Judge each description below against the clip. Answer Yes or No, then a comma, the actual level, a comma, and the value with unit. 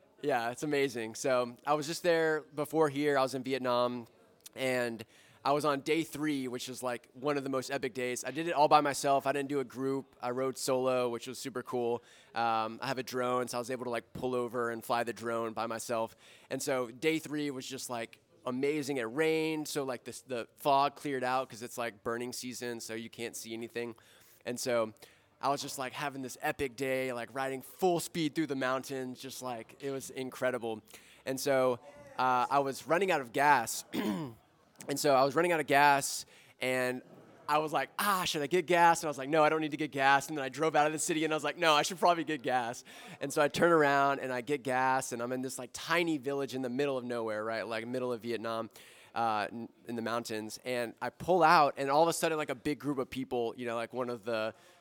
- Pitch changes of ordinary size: Yes, average, 3.2 semitones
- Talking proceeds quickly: Yes, fast, 240 wpm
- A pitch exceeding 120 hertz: Yes, low, 130 Hz